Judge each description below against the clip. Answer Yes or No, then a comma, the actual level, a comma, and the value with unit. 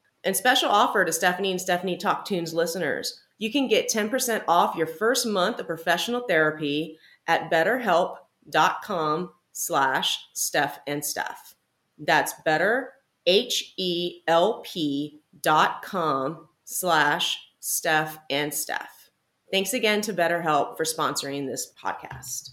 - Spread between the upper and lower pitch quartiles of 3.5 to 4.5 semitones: Yes, average, 3.8 semitones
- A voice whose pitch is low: No, medium, 170 Hz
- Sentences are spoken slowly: Yes, slow, 110 wpm